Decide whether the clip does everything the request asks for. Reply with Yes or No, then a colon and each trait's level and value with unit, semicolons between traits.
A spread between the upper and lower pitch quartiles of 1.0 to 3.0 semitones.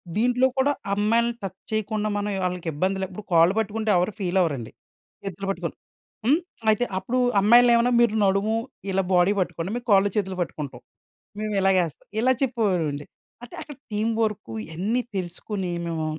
No: average, 3.8 semitones